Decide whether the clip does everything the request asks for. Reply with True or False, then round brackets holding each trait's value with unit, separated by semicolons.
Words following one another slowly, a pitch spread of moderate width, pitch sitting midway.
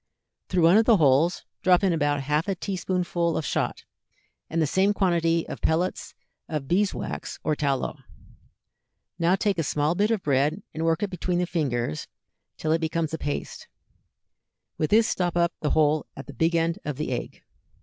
False (190 wpm; 3.3 semitones; 165 Hz)